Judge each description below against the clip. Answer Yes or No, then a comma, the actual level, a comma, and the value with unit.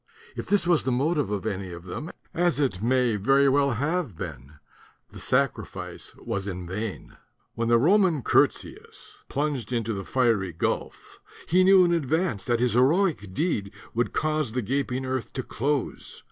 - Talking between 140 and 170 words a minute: Yes, average, 165 wpm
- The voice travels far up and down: Yes, wide, 6.7 semitones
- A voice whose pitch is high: No, low, 125 Hz